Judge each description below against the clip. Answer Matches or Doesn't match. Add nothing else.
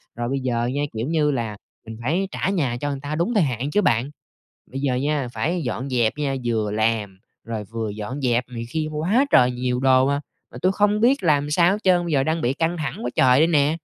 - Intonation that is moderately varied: Matches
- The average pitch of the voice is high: Doesn't match